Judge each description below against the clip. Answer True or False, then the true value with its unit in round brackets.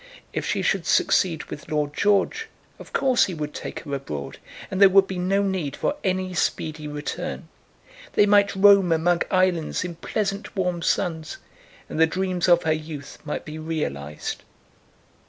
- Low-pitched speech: False (175 Hz)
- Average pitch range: True (3.6 semitones)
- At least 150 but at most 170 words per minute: True (165 wpm)